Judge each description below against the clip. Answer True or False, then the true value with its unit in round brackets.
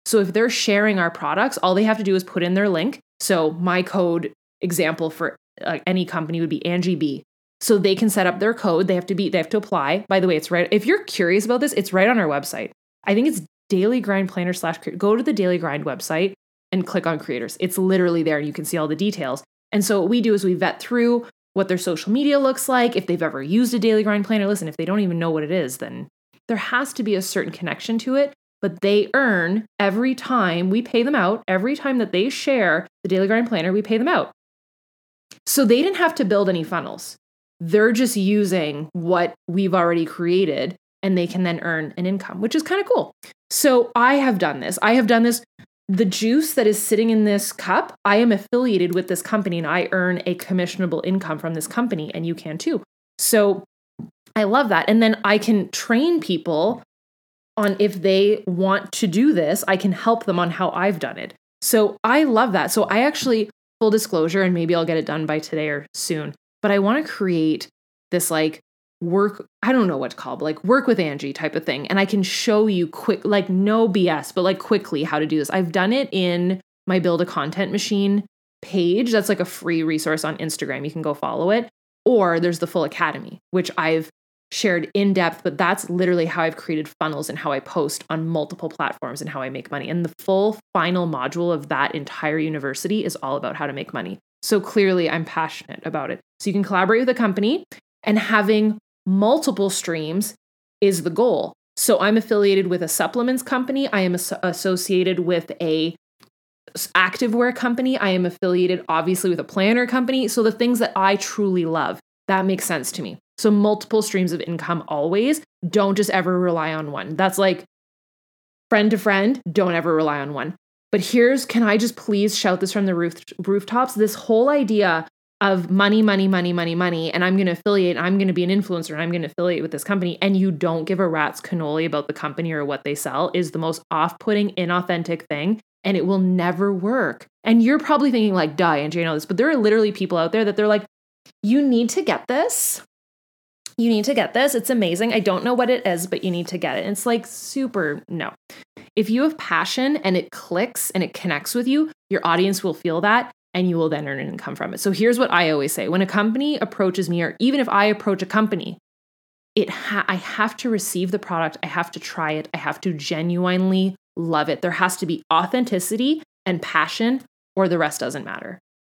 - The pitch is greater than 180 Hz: True (190 Hz)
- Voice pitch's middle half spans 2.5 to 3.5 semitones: False (4.1 semitones)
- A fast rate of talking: True (225 wpm)